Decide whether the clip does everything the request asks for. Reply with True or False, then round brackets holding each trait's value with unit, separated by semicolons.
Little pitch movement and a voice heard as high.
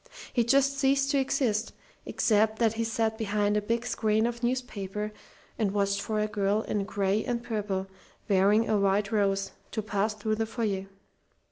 True (2.3 semitones; 215 Hz)